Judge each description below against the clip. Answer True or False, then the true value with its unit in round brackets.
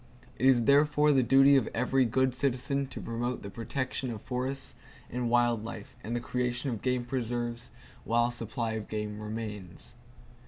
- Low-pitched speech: True (120 Hz)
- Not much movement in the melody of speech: True (2.3 semitones)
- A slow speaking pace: False (170 wpm)